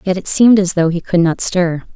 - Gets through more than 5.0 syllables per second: Yes, 5.6 syllables/s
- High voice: No, medium, 180 Hz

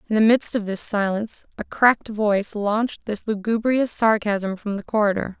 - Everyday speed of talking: Yes, average, 180 wpm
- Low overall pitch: No, high, 215 Hz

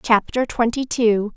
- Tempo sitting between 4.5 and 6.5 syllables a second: No, 4.0 syllables/s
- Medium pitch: No, high, 230 Hz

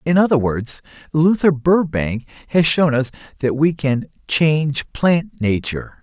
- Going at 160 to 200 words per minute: No, average, 140 wpm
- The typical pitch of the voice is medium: Yes, medium, 145 Hz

